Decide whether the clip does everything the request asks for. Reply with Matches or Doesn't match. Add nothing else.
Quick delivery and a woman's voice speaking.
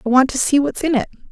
Matches